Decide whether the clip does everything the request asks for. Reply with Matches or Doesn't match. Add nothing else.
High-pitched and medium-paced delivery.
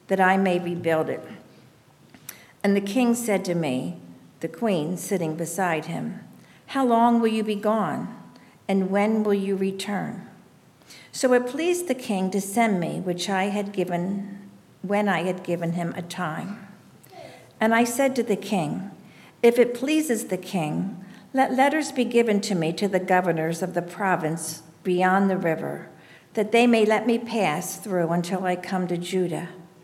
Matches